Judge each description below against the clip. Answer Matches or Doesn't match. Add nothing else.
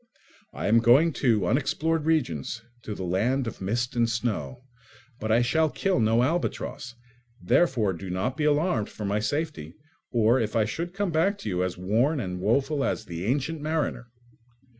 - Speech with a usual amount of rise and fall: Doesn't match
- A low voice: Matches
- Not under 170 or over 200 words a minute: Matches